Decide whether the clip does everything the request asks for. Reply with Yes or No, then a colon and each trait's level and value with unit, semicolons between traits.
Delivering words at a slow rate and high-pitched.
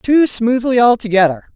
Yes: slow, 115 wpm; high, 230 Hz